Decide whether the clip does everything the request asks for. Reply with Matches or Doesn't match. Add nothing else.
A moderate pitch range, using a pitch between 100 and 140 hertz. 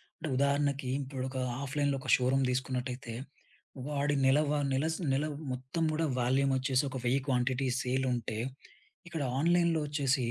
Doesn't match